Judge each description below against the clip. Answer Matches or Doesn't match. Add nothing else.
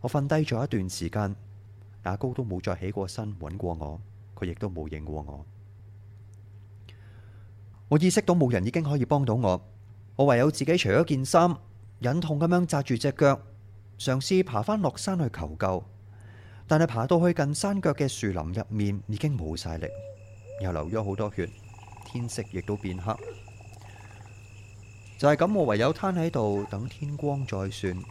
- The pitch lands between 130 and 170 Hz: Doesn't match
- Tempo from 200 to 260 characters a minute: Matches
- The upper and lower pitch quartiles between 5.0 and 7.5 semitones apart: Matches